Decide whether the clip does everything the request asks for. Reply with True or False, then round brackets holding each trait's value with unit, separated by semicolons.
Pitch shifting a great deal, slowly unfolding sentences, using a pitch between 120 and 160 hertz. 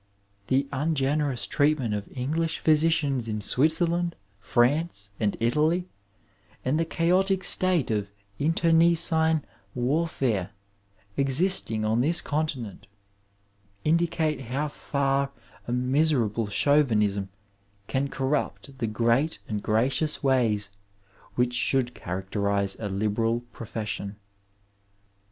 True (5.9 semitones; 100 wpm; 135 Hz)